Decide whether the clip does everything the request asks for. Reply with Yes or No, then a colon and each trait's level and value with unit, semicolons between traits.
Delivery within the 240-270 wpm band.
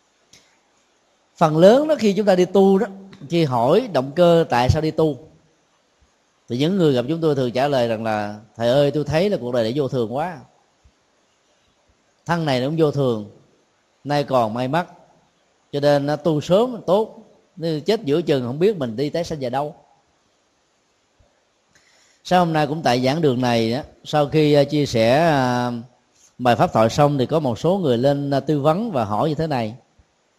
No: average, 190 wpm